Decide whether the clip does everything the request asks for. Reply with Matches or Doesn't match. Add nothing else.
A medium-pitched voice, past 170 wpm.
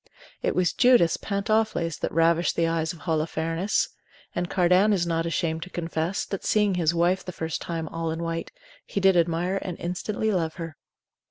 Matches